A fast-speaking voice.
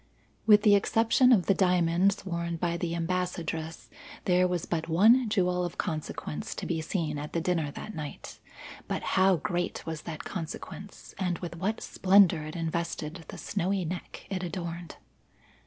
No: average, 160 wpm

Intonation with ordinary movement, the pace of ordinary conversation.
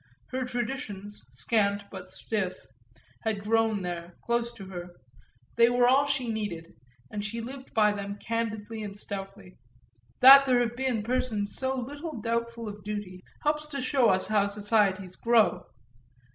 Yes: average, 3.4 semitones; average, 150 wpm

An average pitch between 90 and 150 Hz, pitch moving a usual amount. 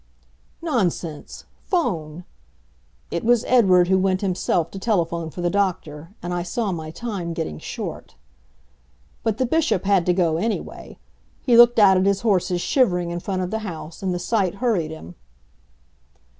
No: medium, 185 Hz; average, 4.1 semitones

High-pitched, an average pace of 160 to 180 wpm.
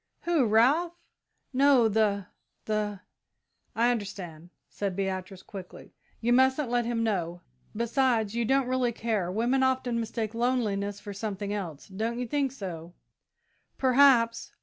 No: high, 225 Hz; slow, 135 wpm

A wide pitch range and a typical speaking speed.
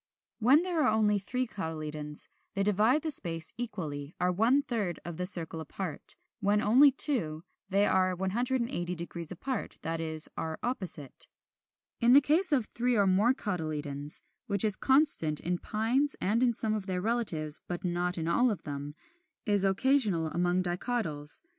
Yes: wide, 6.5 semitones; average, 160 wpm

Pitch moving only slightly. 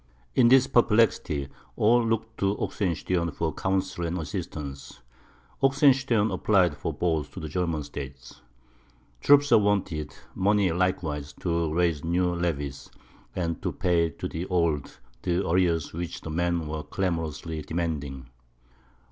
No: average, 3.8 semitones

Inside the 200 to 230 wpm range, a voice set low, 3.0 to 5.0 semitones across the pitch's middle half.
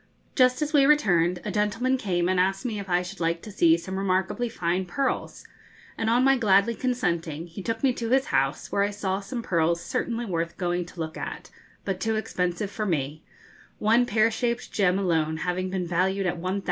No: fast, 205 wpm; high, 190 Hz; average, 4.5 semitones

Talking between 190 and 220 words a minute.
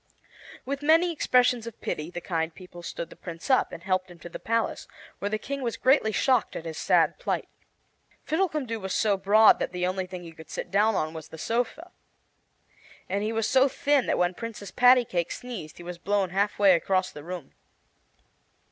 Yes: average, 200 wpm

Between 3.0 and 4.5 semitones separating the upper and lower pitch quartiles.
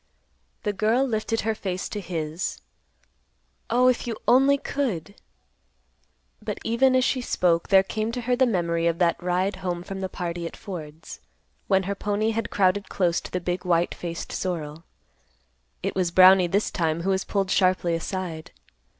Yes: average, 3.9 semitones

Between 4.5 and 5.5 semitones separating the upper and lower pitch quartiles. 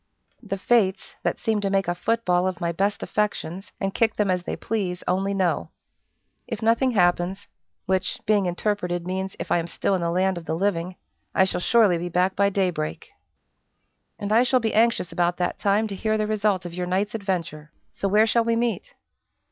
No: average, 3.2 semitones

